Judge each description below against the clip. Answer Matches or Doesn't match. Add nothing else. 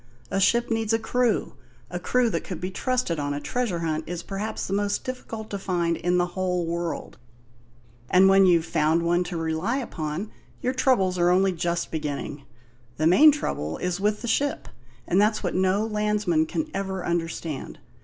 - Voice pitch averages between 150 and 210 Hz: Matches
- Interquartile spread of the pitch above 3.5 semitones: Matches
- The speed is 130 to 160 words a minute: Doesn't match